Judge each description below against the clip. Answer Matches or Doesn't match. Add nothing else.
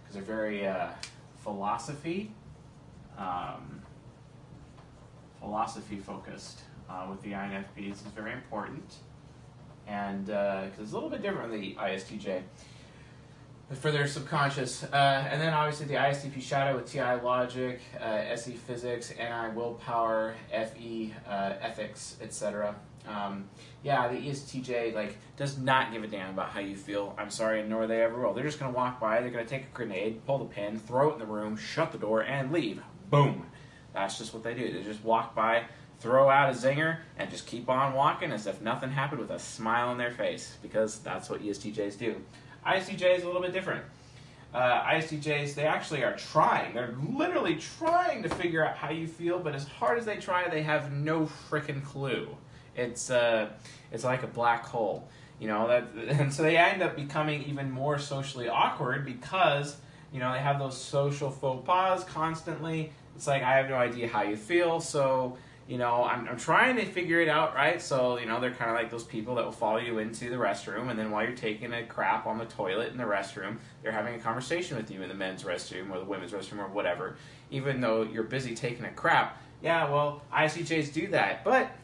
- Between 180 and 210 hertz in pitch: Doesn't match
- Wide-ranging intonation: Doesn't match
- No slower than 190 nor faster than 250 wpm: Matches